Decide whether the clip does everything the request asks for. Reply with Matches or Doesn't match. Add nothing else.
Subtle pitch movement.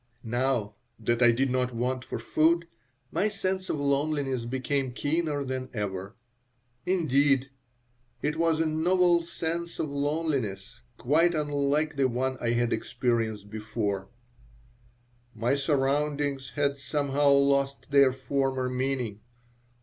Doesn't match